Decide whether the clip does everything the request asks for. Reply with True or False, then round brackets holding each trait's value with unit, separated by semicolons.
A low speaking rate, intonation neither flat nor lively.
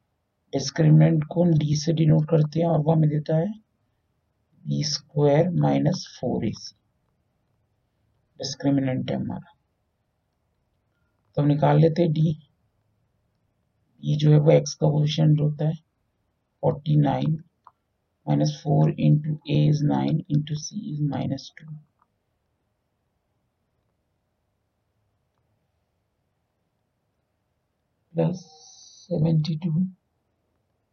False (40 wpm; 6.8 semitones)